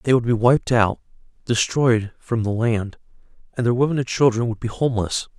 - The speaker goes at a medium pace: Yes, average, 190 wpm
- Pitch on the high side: No, low, 120 Hz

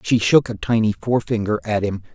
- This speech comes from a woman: No, male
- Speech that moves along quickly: No, average, 195 wpm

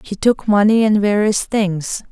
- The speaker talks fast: No, average, 170 wpm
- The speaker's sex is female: Yes, female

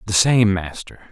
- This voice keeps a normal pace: Yes, average, 160 wpm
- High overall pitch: No, low, 100 Hz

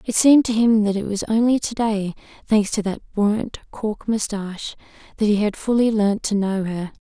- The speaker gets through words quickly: No, average, 195 wpm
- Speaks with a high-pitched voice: Yes, high, 210 Hz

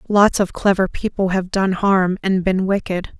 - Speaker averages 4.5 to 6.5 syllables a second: No, 4.3 syllables/s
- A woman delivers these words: Yes, female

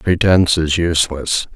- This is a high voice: No, very low, 85 Hz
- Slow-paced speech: Yes, slow, 115 wpm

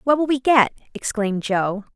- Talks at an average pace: Yes, average, 185 wpm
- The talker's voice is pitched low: No, high, 230 Hz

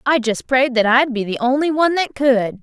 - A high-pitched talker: Yes, very high, 255 Hz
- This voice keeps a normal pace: No, fast, 250 wpm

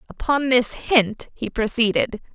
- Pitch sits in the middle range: No, high, 235 Hz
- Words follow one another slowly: Yes, slow, 130 wpm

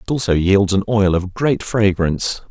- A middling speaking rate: Yes, average, 190 wpm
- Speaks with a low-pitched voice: Yes, low, 100 Hz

